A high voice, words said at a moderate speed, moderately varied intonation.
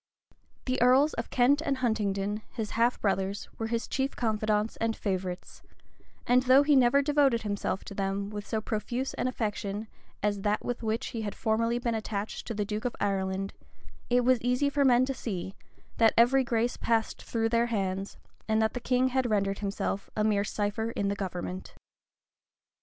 Yes: high, 225 Hz; average, 180 wpm; average, 3.4 semitones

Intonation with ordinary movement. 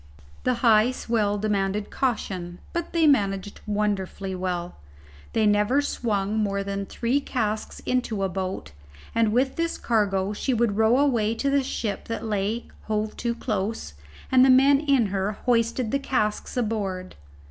Yes: average, 3.8 semitones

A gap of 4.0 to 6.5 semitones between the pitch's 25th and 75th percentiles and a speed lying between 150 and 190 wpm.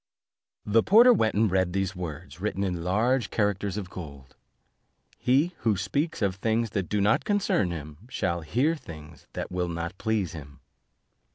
Yes: average, 4.5 semitones; average, 165 wpm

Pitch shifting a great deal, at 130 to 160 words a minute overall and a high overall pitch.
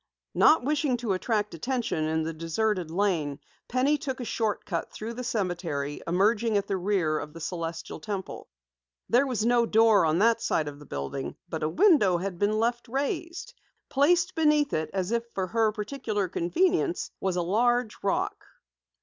No: wide, 6.2 semitones; average, 175 wpm; high, 210 Hz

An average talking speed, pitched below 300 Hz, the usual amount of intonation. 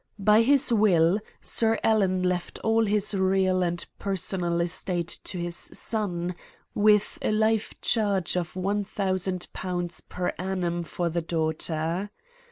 No: slow, 125 wpm; medium, 185 Hz; average, 3.1 semitones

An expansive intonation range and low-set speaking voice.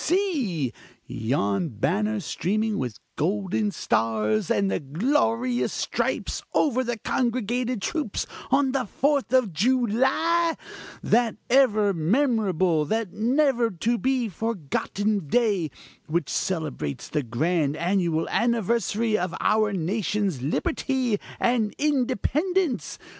No: wide, 6.6 semitones; high, 215 Hz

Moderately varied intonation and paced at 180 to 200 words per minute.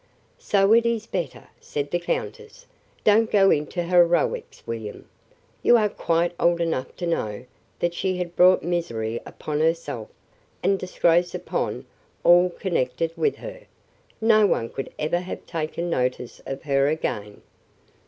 No: average, 4.3 semitones; average, 145 wpm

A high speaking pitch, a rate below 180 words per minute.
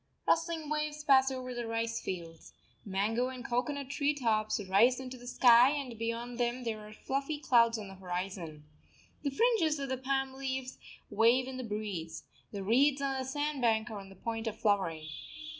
No: high, 245 Hz; average, 185 wpm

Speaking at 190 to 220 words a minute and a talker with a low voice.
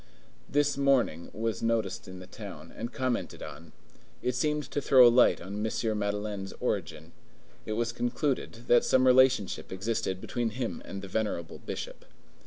No: average, 160 wpm; low, 115 Hz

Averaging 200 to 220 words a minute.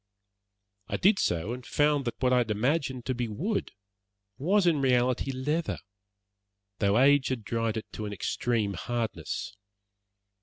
No: average, 150 wpm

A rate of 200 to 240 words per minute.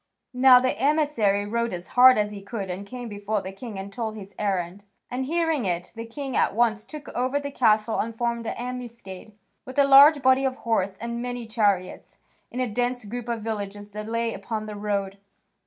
Yes: fast, 205 wpm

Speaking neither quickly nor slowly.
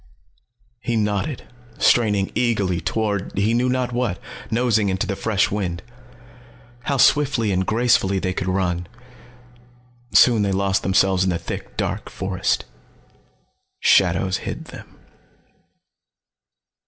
No: slow, 115 wpm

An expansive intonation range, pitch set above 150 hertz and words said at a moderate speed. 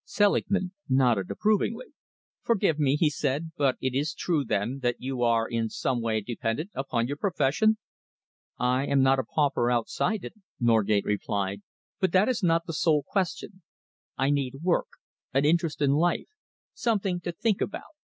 No: wide, 6.4 semitones; medium, 140 Hz; average, 160 wpm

